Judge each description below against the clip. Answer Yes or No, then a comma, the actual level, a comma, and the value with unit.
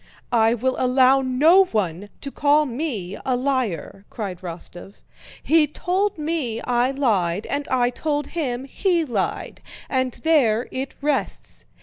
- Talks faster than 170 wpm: No, slow, 135 wpm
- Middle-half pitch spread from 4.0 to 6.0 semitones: Yes, average, 4.9 semitones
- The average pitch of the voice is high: Yes, very high, 260 Hz